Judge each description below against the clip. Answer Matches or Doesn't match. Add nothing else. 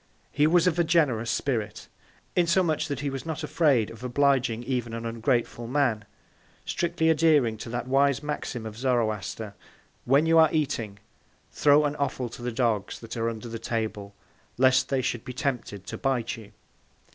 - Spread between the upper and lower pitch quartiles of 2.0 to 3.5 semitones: Doesn't match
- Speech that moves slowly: Doesn't match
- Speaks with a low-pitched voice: Matches